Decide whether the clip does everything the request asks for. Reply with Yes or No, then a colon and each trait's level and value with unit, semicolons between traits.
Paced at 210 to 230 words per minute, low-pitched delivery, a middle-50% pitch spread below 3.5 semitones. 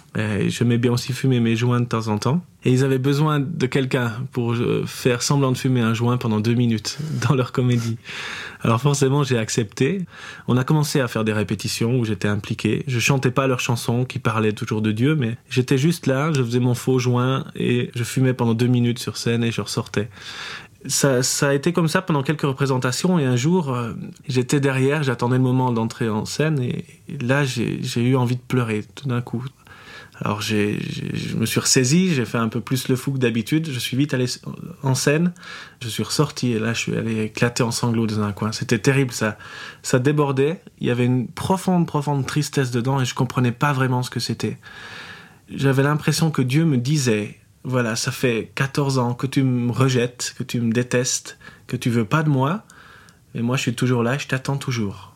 Yes: average, 215 wpm; low, 130 Hz; average, 3.0 semitones